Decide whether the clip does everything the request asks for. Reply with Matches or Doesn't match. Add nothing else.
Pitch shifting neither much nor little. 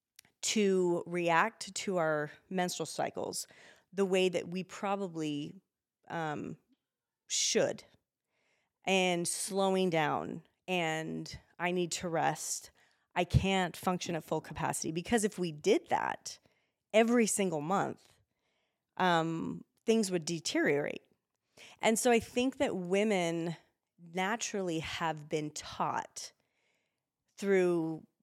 Matches